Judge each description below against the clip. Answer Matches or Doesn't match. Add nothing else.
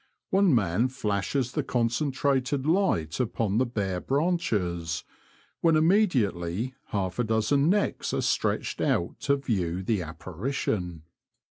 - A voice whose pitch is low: Matches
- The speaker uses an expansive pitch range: Matches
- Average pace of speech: Doesn't match